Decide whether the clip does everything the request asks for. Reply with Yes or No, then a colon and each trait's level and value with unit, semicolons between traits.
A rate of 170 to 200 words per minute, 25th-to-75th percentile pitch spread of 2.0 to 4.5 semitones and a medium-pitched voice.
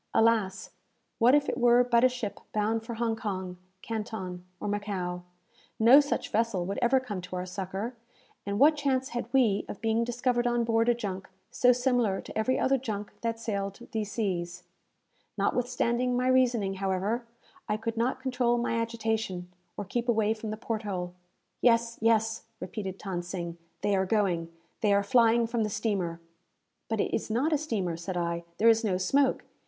No: average, 180 wpm; average, 3.6 semitones; high, 225 Hz